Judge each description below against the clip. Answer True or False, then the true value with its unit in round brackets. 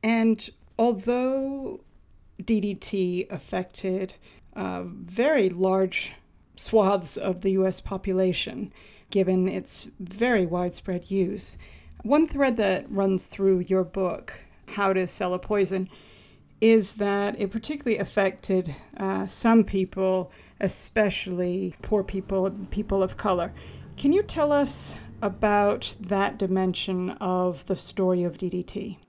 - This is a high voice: True (195 Hz)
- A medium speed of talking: False (115 wpm)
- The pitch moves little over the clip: True (2.1 semitones)